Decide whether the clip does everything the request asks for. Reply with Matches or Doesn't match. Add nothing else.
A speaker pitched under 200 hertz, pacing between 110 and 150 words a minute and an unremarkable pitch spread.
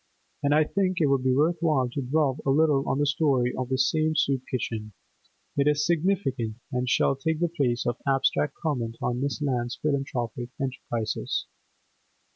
Doesn't match